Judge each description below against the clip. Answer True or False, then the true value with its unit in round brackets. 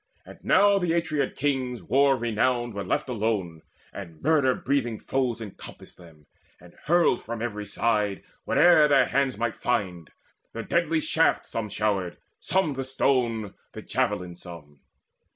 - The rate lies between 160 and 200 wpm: False (150 wpm)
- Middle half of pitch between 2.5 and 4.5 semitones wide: False (5.4 semitones)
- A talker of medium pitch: False (120 Hz)